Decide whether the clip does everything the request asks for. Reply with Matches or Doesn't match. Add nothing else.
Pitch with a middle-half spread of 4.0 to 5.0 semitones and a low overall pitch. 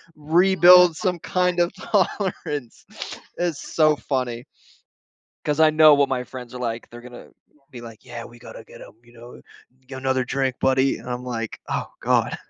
Matches